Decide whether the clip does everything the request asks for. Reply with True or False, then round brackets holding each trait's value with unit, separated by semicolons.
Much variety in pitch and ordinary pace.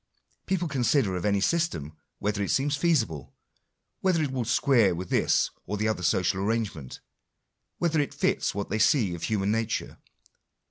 True (6.8 semitones; 160 wpm)